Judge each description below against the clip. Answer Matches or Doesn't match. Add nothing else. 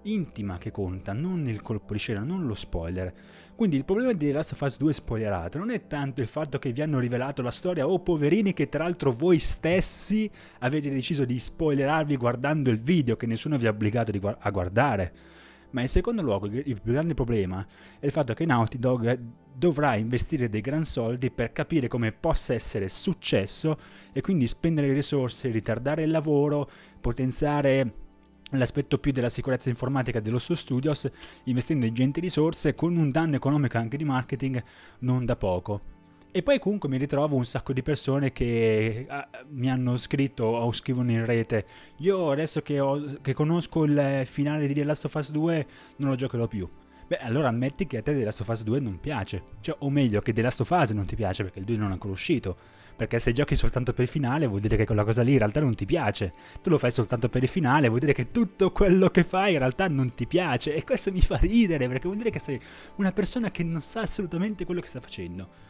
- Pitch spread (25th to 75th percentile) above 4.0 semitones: Matches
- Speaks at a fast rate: Matches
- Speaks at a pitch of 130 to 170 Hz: Matches